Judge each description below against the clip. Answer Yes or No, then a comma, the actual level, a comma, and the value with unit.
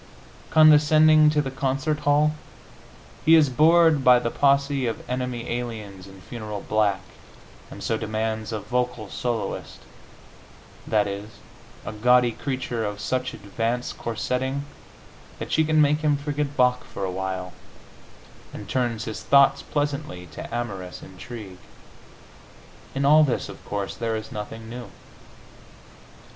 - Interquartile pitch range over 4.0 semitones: Yes, average, 4.8 semitones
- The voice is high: No, low, 125 Hz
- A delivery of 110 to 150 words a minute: Yes, slow, 135 wpm